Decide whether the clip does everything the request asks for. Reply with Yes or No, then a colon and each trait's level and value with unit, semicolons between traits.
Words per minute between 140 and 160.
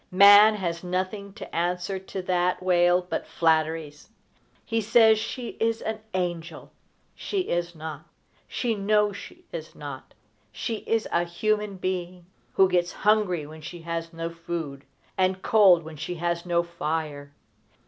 Yes: average, 150 wpm